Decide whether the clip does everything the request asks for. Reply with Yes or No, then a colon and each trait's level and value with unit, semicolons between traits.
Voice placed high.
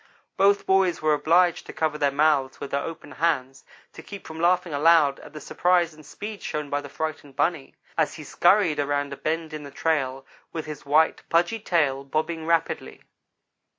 No: medium, 155 Hz